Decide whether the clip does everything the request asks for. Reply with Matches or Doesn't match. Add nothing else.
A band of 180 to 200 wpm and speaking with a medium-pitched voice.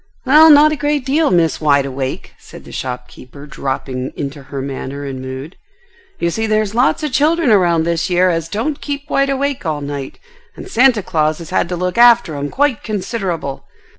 Matches